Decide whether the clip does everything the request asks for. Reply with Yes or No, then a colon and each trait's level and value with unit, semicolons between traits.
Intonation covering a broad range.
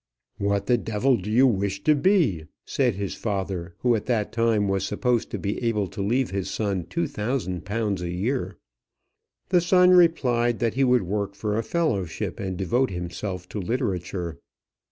No: average, 4.4 semitones